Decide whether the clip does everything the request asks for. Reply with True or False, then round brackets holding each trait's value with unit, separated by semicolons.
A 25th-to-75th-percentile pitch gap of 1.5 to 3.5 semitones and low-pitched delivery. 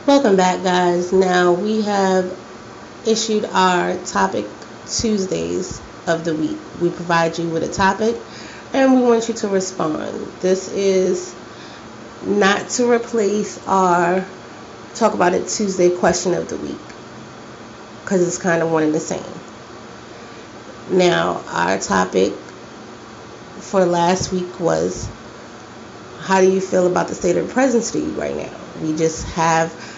False (2.8 semitones; 185 Hz)